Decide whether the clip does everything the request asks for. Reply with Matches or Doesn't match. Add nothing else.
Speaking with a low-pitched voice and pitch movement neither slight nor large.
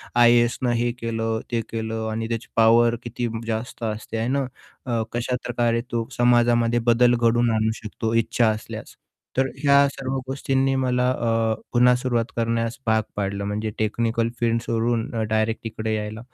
Doesn't match